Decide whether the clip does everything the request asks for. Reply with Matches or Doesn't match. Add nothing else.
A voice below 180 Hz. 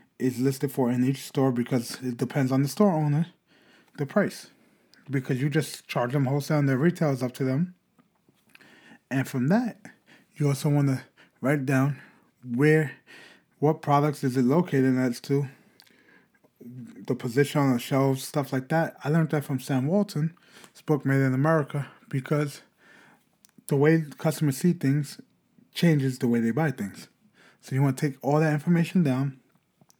Matches